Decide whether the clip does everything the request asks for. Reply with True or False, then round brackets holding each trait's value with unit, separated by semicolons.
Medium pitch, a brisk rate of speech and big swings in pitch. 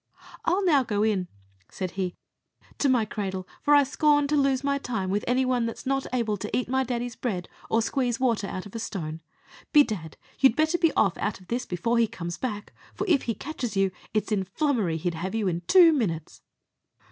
False (230 Hz; 215 wpm; 5.8 semitones)